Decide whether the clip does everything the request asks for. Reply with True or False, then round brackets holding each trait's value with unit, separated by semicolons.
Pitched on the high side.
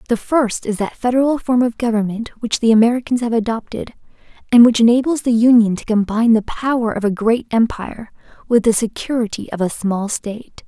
True (230 Hz)